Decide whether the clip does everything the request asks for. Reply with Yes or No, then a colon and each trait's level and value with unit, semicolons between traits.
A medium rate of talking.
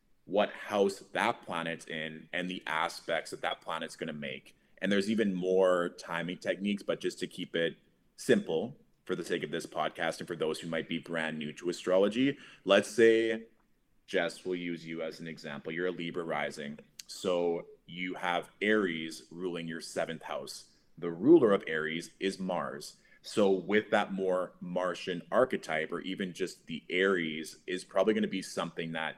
Yes: average, 180 wpm